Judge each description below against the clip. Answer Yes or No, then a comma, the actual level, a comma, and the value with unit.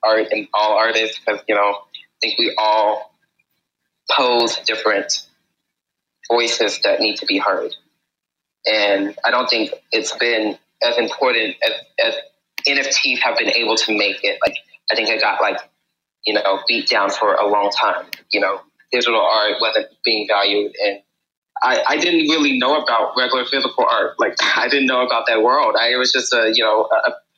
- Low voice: Yes, low, 125 Hz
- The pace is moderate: Yes, average, 180 wpm